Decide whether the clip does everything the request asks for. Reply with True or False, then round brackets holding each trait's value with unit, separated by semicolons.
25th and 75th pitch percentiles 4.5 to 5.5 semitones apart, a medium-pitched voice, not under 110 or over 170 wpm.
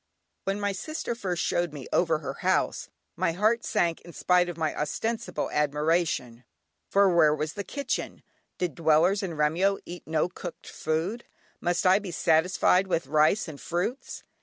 False (3.8 semitones; 175 Hz; 160 wpm)